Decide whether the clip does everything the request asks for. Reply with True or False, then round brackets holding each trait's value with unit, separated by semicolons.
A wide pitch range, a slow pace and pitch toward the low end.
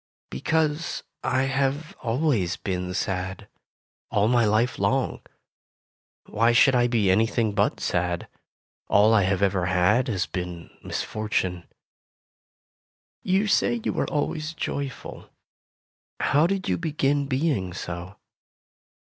True (7.2 semitones; 120 wpm; 115 Hz)